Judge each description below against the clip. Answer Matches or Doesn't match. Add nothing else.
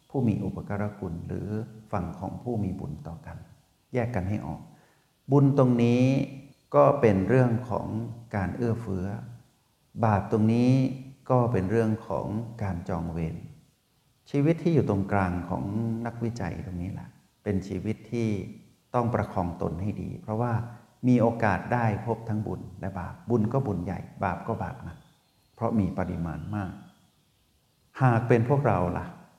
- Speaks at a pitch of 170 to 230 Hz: Doesn't match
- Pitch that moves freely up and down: Doesn't match